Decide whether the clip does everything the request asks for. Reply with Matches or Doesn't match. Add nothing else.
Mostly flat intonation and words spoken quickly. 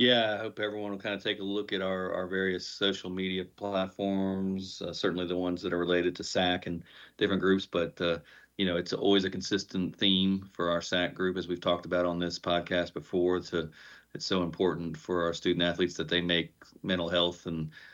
Matches